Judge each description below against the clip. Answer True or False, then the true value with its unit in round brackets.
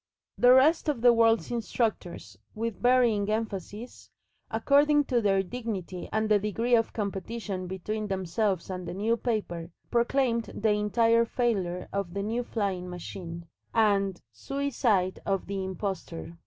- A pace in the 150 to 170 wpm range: False (140 wpm)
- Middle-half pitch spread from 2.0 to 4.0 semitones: True (3.6 semitones)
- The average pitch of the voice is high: True (210 Hz)